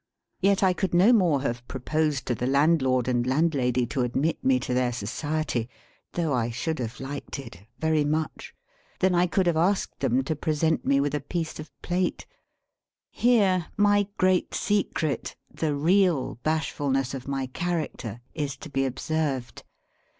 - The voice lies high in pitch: No, medium, 150 Hz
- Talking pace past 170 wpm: No, average, 160 wpm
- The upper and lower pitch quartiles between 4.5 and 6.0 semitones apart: Yes, average, 4.8 semitones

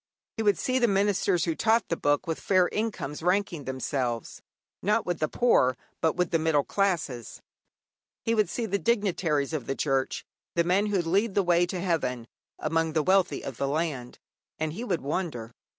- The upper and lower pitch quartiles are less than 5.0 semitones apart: No, wide, 5.4 semitones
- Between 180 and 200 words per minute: Yes, average, 185 wpm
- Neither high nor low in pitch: Yes, medium, 170 Hz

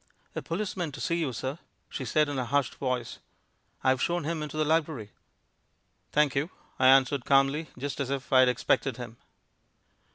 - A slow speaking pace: No, average, 175 wpm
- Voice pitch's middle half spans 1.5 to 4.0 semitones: Yes, average, 3.1 semitones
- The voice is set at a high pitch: No, medium, 140 Hz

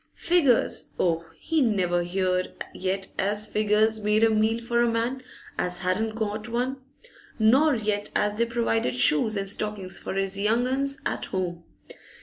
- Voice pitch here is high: Yes, high, 215 Hz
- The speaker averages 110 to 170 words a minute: Yes, average, 155 wpm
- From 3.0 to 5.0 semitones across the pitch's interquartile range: Yes, average, 3.4 semitones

